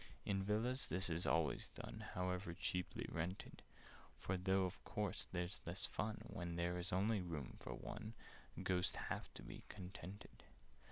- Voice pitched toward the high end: No, very low, 90 Hz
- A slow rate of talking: No, average, 160 wpm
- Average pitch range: No, narrow, 2.1 semitones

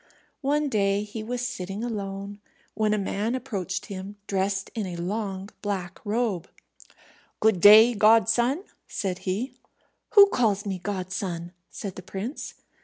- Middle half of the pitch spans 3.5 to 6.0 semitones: No, average, 2.9 semitones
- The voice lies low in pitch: No, high, 205 Hz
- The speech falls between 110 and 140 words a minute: Yes, slow, 135 wpm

